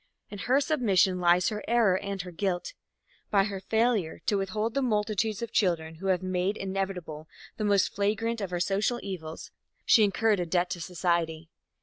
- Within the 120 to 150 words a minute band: No, average, 180 wpm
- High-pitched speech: Yes, high, 195 Hz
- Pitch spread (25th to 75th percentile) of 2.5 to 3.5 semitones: Yes, average, 3.2 semitones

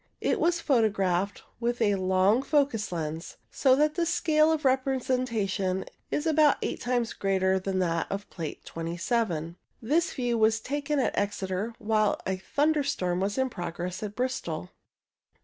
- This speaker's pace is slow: No, average, 155 wpm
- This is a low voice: No, high, 220 Hz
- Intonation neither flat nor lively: No, wide, 6.1 semitones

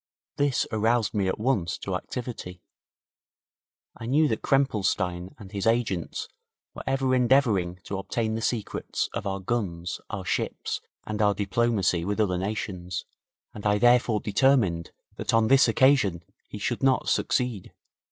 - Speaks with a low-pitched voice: Yes, low, 110 Hz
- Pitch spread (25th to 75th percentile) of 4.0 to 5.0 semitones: Yes, average, 4.3 semitones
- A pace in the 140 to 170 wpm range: Yes, average, 145 wpm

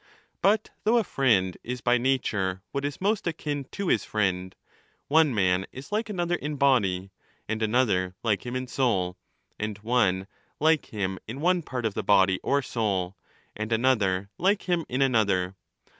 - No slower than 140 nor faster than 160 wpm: No, average, 175 wpm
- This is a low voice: Yes, low, 120 Hz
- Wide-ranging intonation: Yes, wide, 6.9 semitones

